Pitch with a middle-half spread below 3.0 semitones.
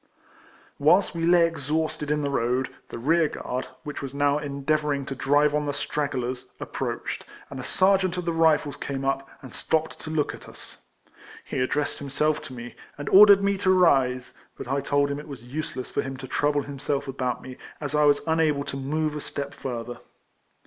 Yes: narrow, 2.5 semitones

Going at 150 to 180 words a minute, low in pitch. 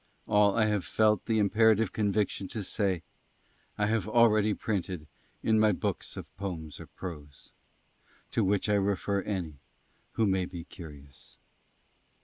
No: average, 140 wpm; low, 100 Hz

